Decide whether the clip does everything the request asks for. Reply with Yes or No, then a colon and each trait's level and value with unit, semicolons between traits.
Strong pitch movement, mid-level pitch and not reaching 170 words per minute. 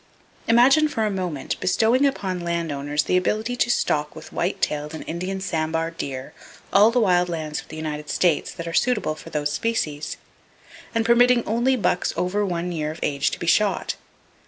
No: wide, 6.0 semitones; medium, 175 Hz; average, 185 wpm